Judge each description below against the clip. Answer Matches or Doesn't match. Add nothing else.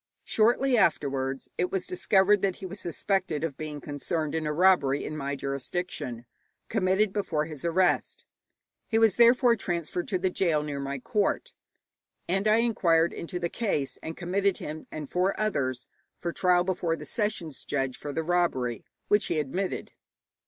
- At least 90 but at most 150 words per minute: Doesn't match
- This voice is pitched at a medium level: Matches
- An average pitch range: Matches